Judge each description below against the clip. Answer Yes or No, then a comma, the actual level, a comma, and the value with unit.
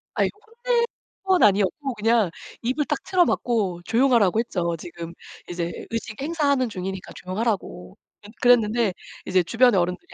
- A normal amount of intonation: No, wide, 5.7 semitones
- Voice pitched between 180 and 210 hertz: No, high, 220 Hz